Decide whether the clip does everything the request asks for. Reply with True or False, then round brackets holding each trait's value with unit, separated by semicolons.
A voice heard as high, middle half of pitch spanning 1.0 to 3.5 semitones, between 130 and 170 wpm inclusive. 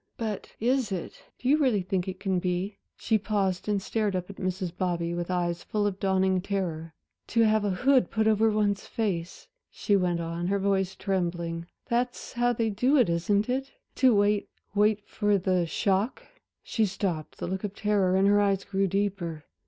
False (195 Hz; 2.9 semitones; 190 wpm)